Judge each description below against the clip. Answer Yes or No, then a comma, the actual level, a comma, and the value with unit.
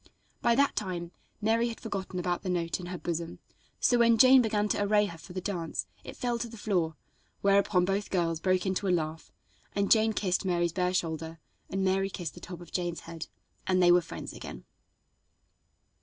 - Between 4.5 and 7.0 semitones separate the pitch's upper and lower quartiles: No, average, 3.2 semitones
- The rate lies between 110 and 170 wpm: No, average, 200 wpm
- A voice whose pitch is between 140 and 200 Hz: Yes, medium, 185 Hz